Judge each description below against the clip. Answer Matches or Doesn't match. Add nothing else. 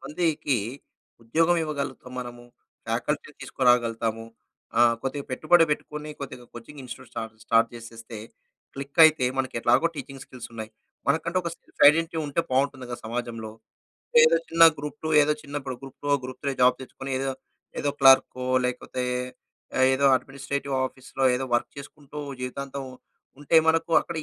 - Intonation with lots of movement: Doesn't match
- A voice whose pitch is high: Doesn't match